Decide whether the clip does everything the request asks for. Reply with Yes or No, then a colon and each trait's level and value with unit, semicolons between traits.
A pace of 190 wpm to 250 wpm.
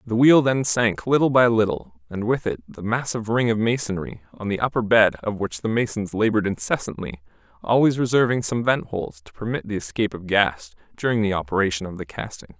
Yes: average, 200 wpm